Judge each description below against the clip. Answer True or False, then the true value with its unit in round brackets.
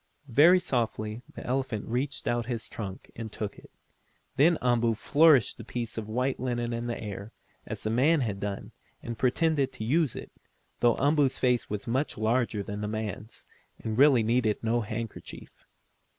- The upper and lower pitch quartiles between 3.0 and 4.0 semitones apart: True (3.3 semitones)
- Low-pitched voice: True (120 Hz)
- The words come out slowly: False (170 wpm)